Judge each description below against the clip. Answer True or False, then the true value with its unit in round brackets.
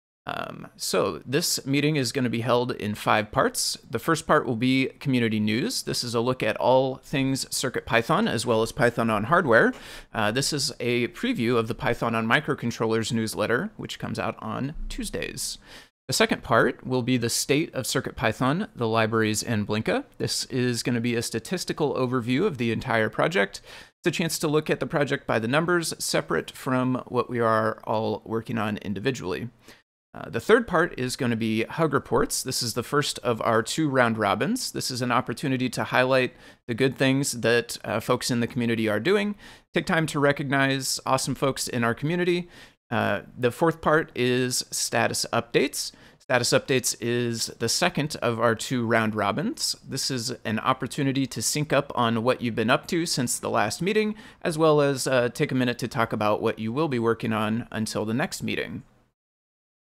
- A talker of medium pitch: False (125 Hz)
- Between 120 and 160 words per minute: False (195 wpm)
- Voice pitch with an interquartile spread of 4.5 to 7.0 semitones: False (3.6 semitones)